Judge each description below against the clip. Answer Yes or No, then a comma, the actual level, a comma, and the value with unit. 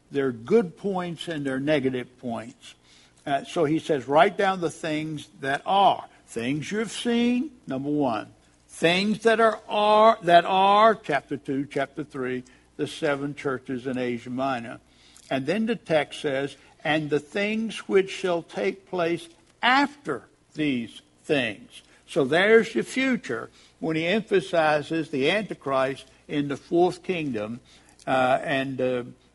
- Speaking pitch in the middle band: Yes, medium, 155 Hz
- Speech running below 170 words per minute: Yes, average, 140 wpm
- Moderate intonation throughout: No, wide, 6.5 semitones